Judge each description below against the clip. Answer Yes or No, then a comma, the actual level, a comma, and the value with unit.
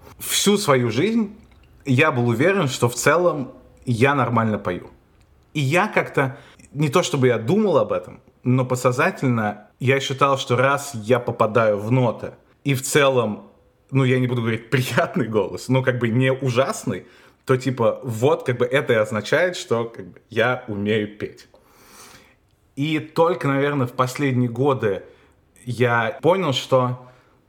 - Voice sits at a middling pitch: No, low, 130 Hz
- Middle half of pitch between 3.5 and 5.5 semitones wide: No, average, 2.8 semitones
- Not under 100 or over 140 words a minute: No, average, 155 wpm